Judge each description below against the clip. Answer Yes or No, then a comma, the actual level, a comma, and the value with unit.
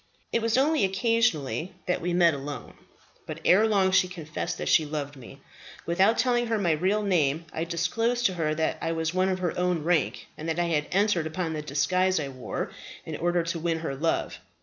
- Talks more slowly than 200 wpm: No, fast, 205 wpm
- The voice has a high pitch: No, medium, 175 Hz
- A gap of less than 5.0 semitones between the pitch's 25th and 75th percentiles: Yes, average, 3.4 semitones